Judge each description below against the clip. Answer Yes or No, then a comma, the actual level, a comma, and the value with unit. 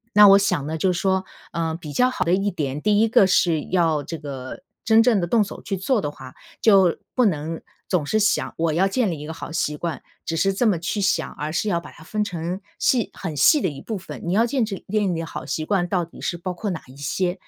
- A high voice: No, medium, 180 Hz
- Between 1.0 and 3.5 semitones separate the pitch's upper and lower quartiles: No, average, 4.1 semitones